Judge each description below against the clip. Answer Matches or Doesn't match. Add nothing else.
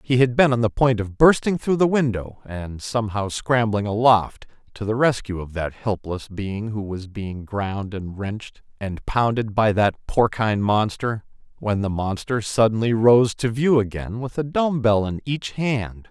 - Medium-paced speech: Matches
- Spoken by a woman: Doesn't match